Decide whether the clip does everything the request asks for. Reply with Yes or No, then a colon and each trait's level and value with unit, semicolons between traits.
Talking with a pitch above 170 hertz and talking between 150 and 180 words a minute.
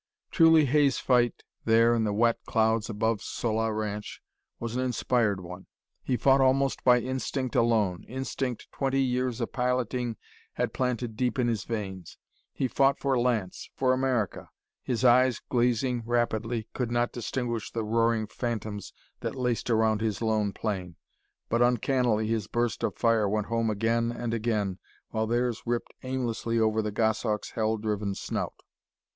No: low, 115 Hz; average, 155 wpm